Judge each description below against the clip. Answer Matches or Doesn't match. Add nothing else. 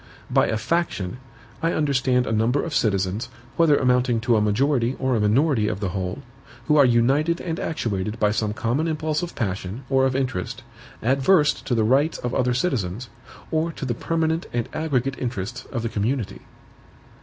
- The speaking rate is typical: Matches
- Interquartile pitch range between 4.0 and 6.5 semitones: Matches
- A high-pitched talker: Doesn't match